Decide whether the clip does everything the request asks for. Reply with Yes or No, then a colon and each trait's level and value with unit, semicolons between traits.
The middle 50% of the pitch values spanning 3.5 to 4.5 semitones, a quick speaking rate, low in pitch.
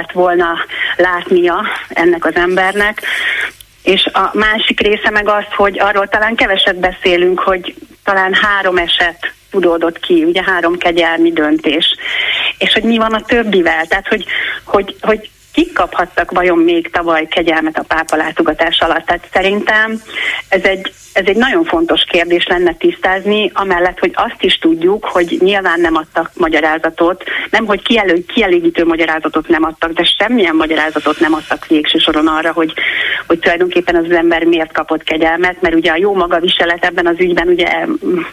No: average, 4.0 semitones; fast, 160 wpm; medium, 180 Hz